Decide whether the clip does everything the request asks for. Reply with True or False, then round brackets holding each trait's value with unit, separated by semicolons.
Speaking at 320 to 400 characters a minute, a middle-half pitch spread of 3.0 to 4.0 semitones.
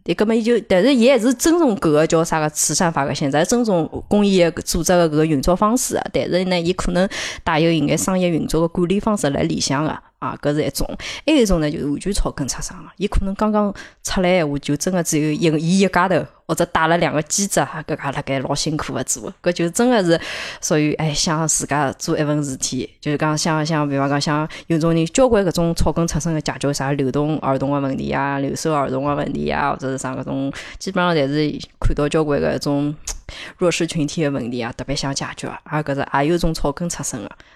True (340 characters per minute; 3.6 semitones)